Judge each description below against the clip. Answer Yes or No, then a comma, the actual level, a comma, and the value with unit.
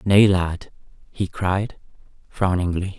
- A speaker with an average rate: No, slow, 100 wpm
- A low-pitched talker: Yes, very low, 90 Hz